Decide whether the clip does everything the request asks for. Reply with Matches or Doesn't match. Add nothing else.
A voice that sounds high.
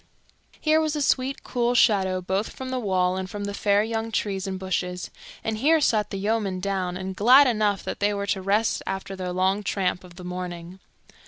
Matches